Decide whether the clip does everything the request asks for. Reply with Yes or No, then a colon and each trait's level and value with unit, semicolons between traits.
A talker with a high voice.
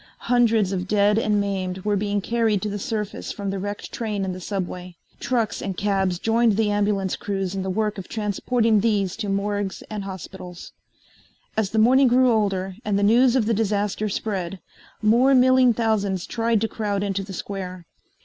Yes: high, 205 Hz